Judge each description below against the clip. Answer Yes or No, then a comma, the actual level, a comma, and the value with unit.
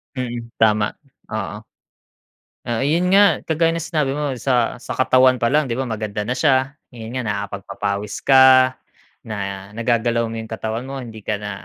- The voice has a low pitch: Yes, low, 120 Hz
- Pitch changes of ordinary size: Yes, average, 3.6 semitones